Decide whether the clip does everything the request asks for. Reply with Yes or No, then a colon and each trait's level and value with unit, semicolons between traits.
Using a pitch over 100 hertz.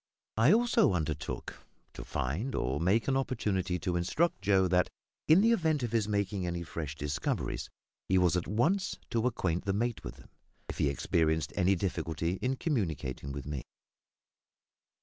No: very low, 95 Hz